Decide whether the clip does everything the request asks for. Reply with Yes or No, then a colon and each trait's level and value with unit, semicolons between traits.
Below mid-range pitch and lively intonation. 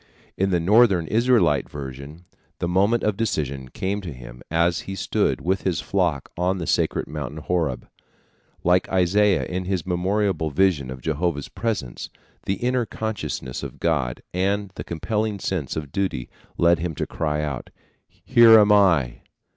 No: very low, 90 Hz; average, 4.8 semitones